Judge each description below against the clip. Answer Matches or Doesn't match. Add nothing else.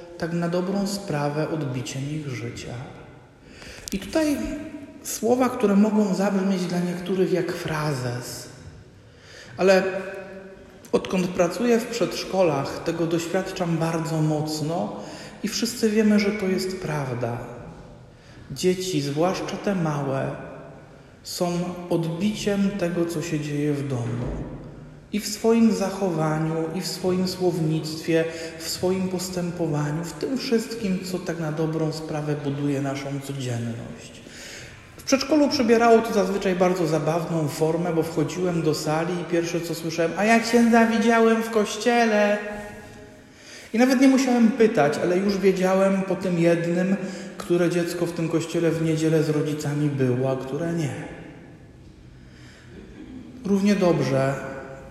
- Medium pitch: Matches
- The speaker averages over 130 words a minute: Doesn't match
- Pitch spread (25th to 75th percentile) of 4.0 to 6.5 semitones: Matches